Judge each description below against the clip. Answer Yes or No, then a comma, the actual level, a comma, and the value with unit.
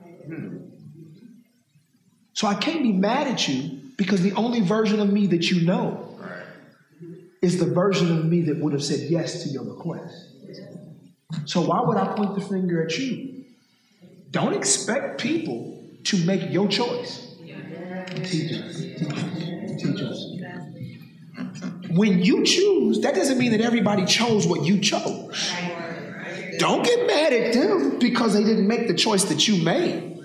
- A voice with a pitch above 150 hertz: Yes, medium, 185 Hz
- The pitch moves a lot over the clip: No, average, 3.8 semitones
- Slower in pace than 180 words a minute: Yes, average, 140 wpm